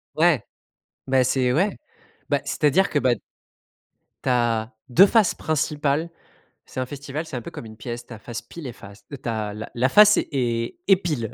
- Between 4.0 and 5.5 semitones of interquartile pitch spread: Yes, average, 5.0 semitones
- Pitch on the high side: No, low, 130 Hz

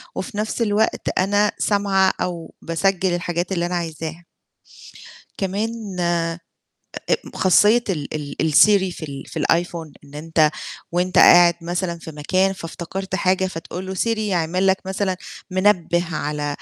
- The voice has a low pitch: No, medium, 180 Hz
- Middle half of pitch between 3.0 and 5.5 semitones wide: No, narrow, 2.6 semitones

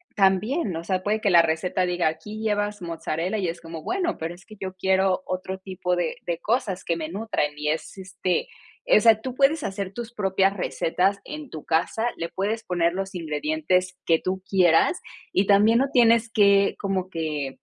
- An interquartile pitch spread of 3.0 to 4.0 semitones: Yes, average, 3.6 semitones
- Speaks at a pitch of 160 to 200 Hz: Yes, high, 190 Hz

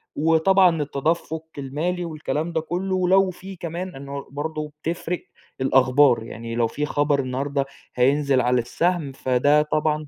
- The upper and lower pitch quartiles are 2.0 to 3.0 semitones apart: No, average, 3.8 semitones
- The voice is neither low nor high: Yes, medium, 150 Hz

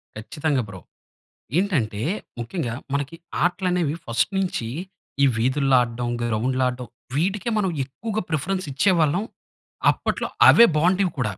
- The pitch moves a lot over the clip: Yes, wide, 7.1 semitones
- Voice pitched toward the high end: No, medium, 145 Hz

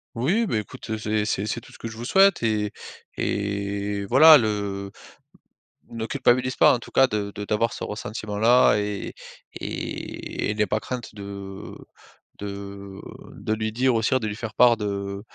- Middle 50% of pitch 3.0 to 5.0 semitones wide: No, narrow, 2.5 semitones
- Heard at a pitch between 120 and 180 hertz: No, low, 110 Hz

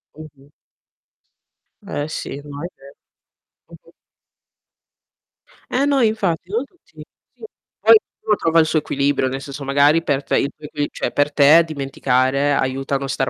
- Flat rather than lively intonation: No, average, 3.2 semitones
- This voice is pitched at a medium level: Yes, medium, 145 Hz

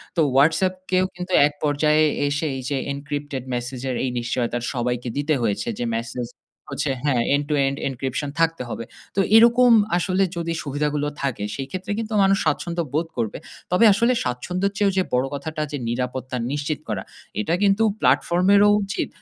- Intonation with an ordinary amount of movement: No, wide, 5.9 semitones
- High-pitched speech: No, medium, 145 Hz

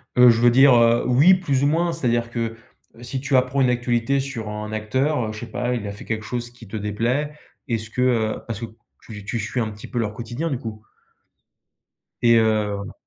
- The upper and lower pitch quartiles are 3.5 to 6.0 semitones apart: No, average, 2.7 semitones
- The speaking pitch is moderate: No, low, 120 Hz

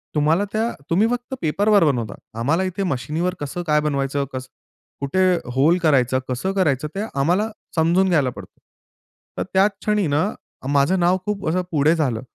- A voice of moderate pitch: Yes, medium, 165 Hz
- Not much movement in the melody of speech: No, average, 5.2 semitones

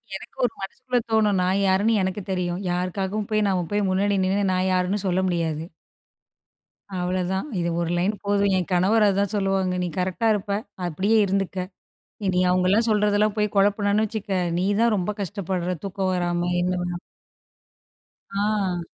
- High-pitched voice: Yes, high, 195 Hz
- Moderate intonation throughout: No, narrow, 2.1 semitones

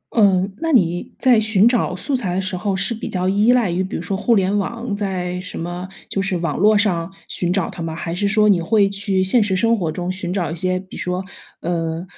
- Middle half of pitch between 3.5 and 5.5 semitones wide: No, average, 2.8 semitones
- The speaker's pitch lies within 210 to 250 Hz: No, high, 190 Hz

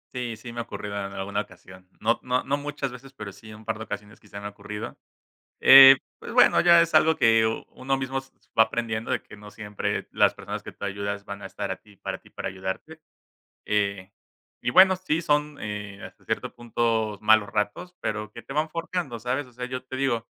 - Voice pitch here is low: Yes, low, 110 Hz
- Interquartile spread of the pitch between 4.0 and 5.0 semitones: Yes, average, 4.5 semitones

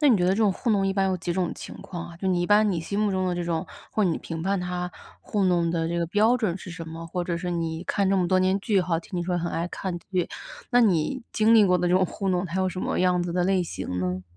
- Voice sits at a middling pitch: Yes, medium, 180 Hz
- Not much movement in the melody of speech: Yes, narrow, 2.1 semitones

